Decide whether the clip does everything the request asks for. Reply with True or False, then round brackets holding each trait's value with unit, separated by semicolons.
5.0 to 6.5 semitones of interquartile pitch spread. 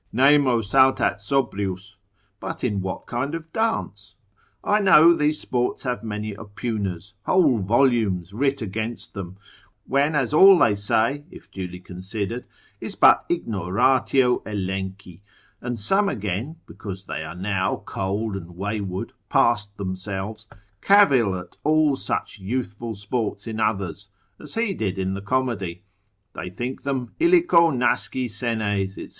True (5.4 semitones)